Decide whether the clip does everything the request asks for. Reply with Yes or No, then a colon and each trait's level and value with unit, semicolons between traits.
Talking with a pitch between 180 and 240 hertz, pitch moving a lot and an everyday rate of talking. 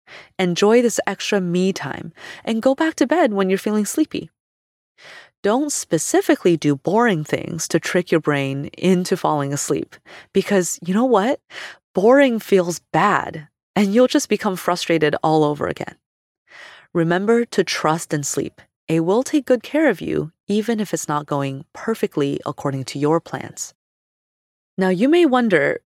Yes: high, 190 Hz; wide, 6.4 semitones; average, 155 wpm